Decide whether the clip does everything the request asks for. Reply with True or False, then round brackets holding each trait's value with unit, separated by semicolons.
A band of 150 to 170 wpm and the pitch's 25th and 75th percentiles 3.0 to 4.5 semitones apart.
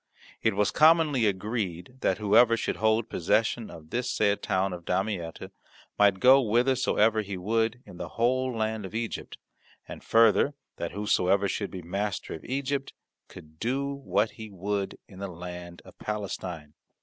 True (160 wpm; 3.9 semitones)